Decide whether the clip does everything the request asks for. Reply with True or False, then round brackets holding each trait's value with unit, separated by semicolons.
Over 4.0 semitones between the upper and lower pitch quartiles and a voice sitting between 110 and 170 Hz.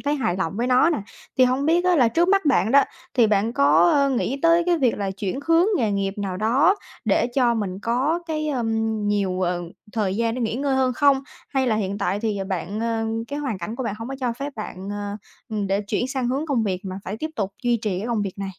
False (5.2 semitones; 230 Hz)